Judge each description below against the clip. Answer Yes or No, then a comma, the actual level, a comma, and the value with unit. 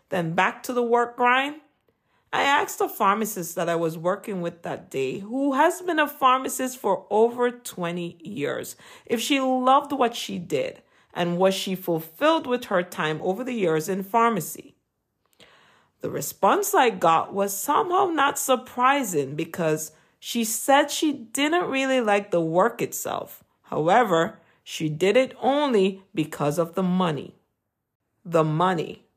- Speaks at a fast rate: No, average, 150 wpm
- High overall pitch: Yes, high, 205 Hz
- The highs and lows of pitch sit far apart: Yes, wide, 7.3 semitones